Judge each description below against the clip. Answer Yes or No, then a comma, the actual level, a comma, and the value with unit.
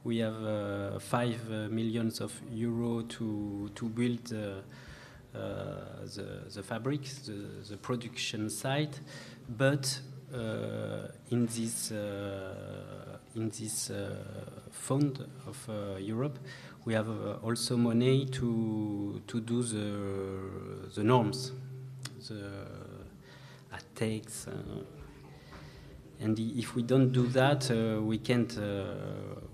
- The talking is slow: Yes, slow, 115 wpm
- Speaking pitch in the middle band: No, low, 115 Hz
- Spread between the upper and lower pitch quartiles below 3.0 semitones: No, average, 3.4 semitones